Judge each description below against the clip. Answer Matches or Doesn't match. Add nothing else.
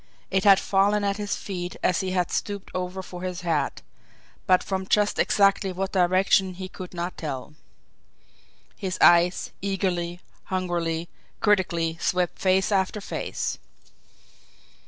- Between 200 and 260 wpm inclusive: Doesn't match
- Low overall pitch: Doesn't match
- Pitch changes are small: Matches